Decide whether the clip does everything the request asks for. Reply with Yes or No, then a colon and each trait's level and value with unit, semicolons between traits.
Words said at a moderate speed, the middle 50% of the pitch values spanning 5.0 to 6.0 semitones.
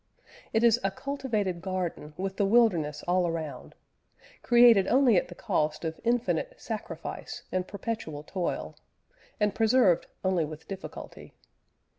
No: slow, 130 wpm; wide, 5.5 semitones